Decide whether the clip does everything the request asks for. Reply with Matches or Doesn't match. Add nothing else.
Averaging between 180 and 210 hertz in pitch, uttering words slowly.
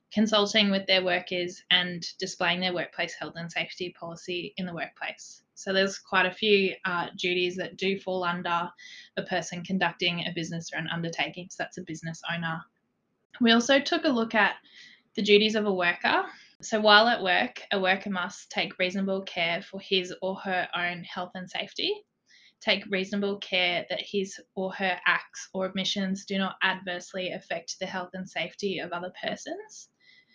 Doesn't match